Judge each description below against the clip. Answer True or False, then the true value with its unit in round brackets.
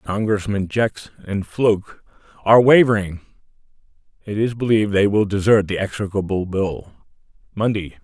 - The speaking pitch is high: False (100 Hz)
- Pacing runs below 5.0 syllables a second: False (5.2 syllables/s)